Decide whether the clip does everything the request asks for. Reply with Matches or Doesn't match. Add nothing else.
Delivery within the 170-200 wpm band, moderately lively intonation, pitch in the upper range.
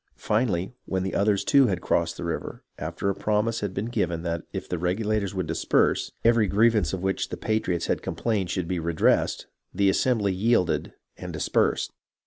Doesn't match